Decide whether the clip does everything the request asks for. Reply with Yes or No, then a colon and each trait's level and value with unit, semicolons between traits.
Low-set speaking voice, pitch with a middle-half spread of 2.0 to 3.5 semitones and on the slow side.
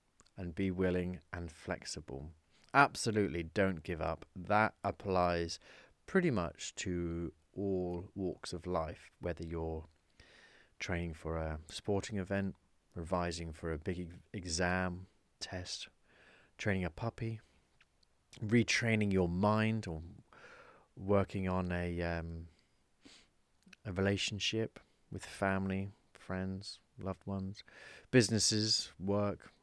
Yes: very low, 90 Hz; average, 2.9 semitones; slow, 105 wpm